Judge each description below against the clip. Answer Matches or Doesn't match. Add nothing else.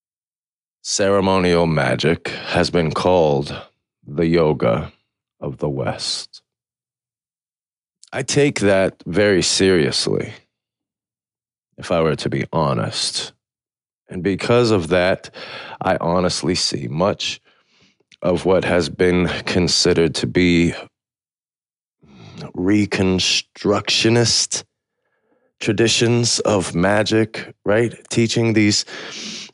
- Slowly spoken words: Matches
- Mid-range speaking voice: Doesn't match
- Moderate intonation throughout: Matches